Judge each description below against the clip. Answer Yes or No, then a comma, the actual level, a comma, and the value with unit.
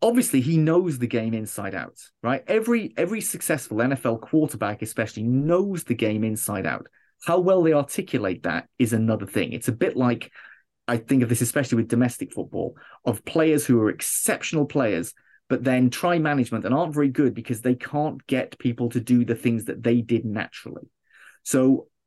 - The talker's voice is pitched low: Yes, low, 125 Hz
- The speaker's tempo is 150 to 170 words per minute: No, average, 180 wpm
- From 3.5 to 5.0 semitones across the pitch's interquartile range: Yes, average, 4.7 semitones